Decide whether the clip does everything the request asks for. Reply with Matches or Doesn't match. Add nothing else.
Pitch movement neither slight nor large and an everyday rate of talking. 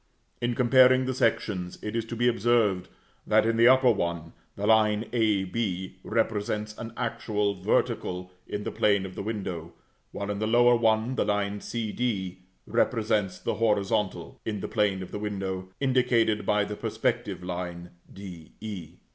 Matches